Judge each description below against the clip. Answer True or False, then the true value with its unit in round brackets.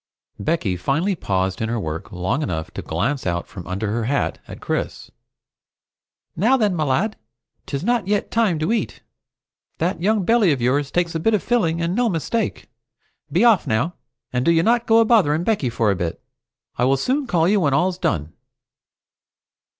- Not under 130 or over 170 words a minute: False (190 wpm)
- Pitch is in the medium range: True (165 Hz)